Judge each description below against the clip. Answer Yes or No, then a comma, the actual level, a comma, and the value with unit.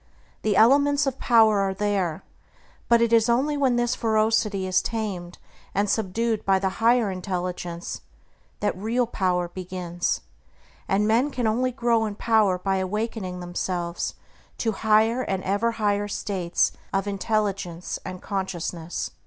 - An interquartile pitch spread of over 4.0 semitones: No, average, 3.7 semitones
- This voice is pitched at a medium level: No, high, 205 Hz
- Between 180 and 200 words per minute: No, average, 140 wpm